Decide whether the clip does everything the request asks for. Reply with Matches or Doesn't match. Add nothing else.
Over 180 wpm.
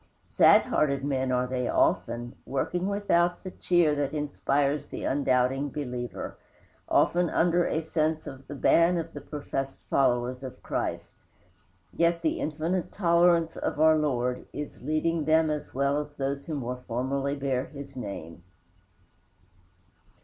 Doesn't match